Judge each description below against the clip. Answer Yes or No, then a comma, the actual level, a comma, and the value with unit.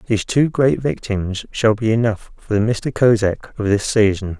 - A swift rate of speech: No, average, 190 wpm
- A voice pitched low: Yes, low, 110 Hz